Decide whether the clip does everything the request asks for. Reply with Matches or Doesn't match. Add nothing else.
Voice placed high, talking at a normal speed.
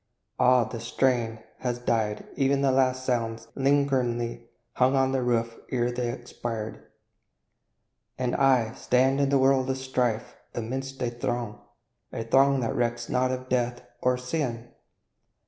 Doesn't match